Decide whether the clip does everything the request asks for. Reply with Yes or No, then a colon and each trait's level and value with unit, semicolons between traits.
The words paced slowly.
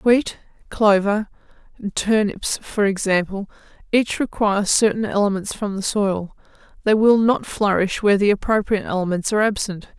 Yes: slow, 130 wpm